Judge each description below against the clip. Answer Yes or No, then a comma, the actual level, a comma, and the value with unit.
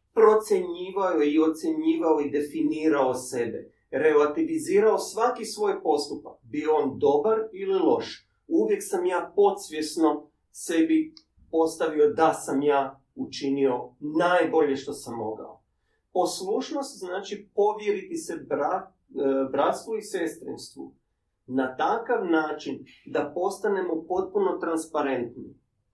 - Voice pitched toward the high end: No, medium, 175 Hz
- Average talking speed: No, slow, 105 wpm